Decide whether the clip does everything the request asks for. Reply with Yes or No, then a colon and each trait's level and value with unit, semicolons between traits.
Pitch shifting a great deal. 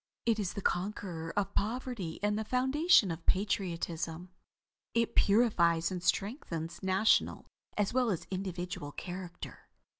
No: average, 4.0 semitones